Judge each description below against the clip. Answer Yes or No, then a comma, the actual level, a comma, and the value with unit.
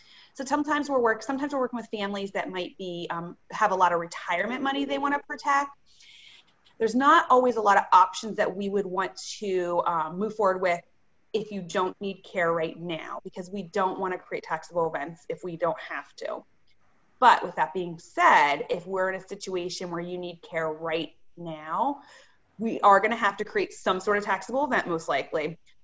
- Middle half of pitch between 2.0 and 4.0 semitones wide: No, average, 5.1 semitones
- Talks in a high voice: Yes, high, 195 Hz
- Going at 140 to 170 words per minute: No, average, 200 wpm